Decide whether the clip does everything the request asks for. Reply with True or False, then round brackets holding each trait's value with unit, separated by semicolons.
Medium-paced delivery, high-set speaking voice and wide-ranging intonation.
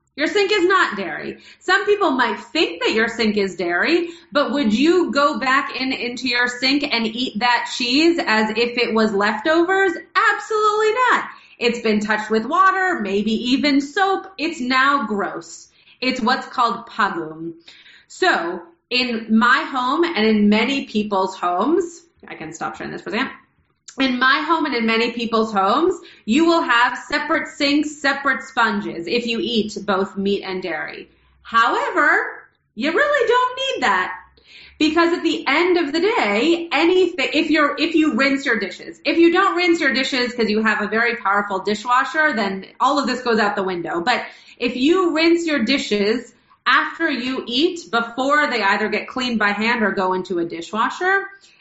True (175 wpm; 260 Hz; 6.8 semitones)